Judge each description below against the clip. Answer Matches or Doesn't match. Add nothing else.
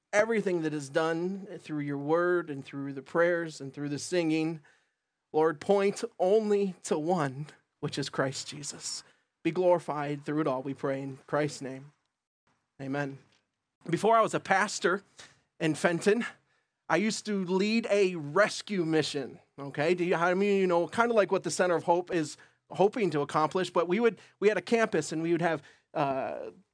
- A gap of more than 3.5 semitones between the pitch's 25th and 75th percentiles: Matches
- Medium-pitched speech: Matches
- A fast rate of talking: Doesn't match